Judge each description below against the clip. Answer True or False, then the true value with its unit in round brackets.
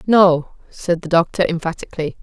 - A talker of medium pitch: True (170 Hz)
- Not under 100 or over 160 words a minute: True (135 wpm)